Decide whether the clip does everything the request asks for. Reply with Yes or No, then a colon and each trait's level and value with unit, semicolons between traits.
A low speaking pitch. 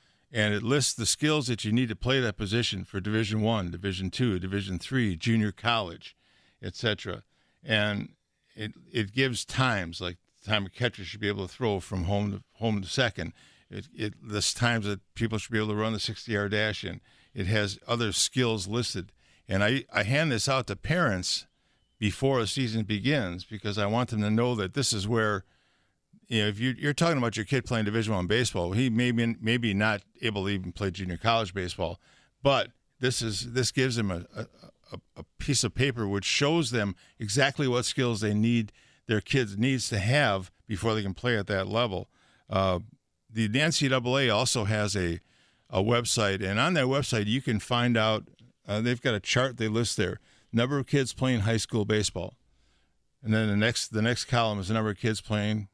Yes: low, 110 Hz